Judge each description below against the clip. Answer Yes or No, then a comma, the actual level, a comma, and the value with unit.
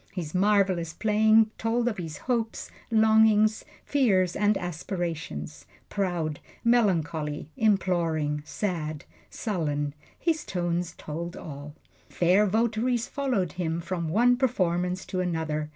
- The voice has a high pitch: No, medium, 180 Hz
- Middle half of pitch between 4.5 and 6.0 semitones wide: Yes, average, 5.1 semitones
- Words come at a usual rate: No, slow, 110 wpm